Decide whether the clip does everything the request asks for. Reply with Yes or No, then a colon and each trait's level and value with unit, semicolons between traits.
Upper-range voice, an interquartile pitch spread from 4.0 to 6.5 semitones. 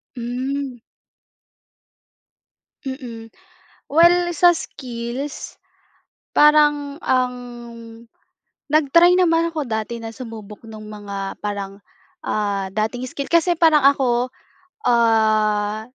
Yes: high, 245 Hz; wide, 5.4 semitones